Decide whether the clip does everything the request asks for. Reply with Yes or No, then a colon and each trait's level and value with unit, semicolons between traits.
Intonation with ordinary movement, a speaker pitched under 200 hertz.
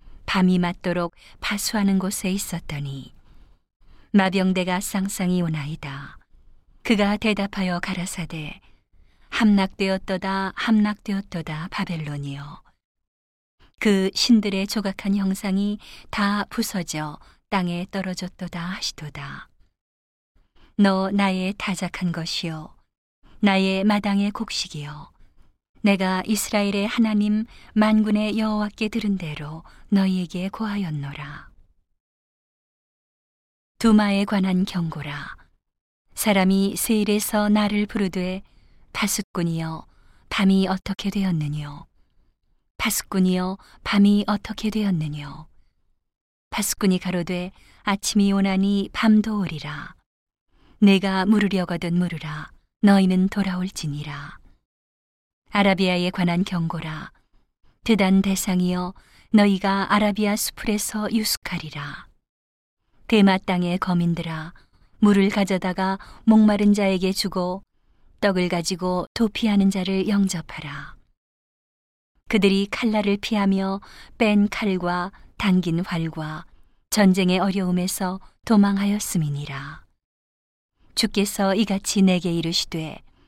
Yes: average, 3.0 semitones; high, 190 Hz